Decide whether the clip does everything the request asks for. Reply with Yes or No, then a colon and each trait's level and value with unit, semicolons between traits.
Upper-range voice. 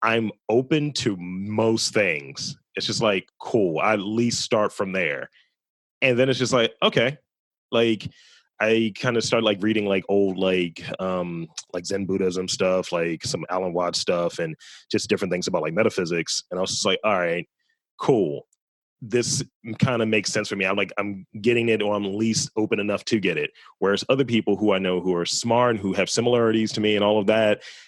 No: low, 105 Hz